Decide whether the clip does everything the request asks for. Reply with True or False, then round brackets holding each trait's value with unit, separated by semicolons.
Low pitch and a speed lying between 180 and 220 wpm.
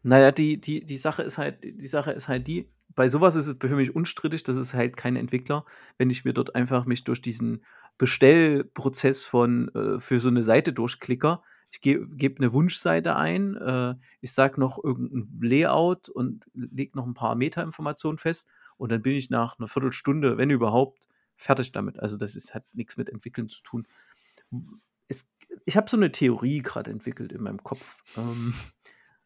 True (130 Hz; 185 wpm)